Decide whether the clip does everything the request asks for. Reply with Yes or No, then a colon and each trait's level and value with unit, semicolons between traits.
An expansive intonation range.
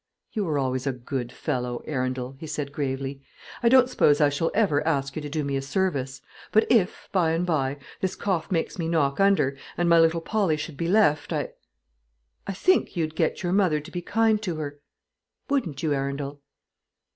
No: average, 4.7 semitones